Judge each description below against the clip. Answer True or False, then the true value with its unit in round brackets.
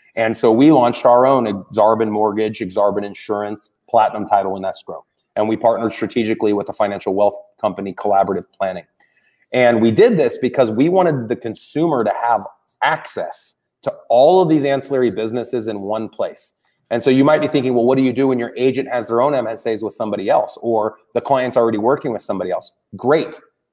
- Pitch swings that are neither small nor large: True (3.1 semitones)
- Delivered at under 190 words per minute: False (195 wpm)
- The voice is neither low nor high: False (115 Hz)